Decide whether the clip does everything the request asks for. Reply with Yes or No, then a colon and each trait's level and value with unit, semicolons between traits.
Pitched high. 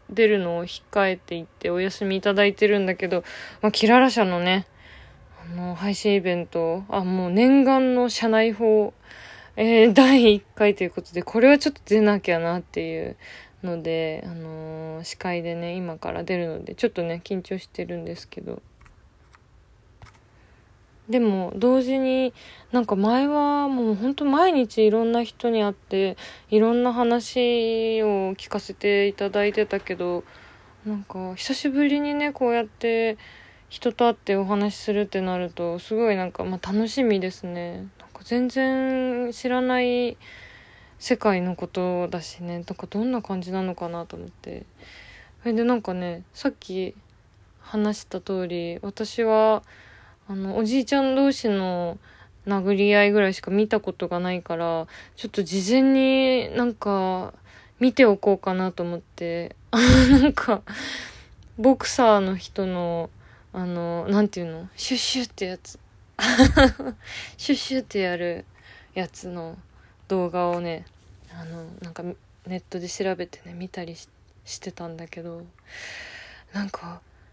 Yes: high, 195 Hz